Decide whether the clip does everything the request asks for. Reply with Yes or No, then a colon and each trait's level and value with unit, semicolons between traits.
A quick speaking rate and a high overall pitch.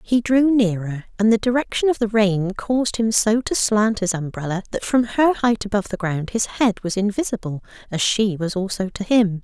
Yes: fast, 210 wpm; high, 210 Hz